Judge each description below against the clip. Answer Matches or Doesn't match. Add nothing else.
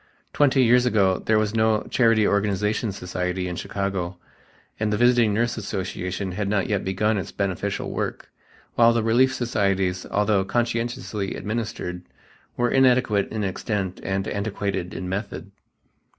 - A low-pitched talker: Matches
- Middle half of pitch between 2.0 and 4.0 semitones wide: Matches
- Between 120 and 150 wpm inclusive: Matches